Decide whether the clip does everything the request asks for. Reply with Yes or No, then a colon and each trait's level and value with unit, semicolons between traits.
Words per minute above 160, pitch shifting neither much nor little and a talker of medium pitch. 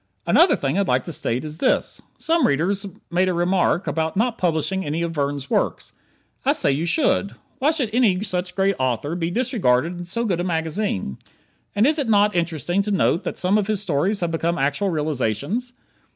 Yes: average, 195 wpm; average, 4.6 semitones; medium, 175 Hz